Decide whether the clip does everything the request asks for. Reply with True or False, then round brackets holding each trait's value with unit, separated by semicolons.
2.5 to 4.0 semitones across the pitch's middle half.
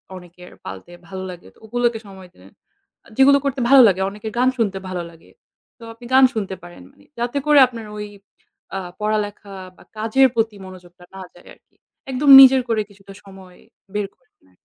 False (4.6 semitones)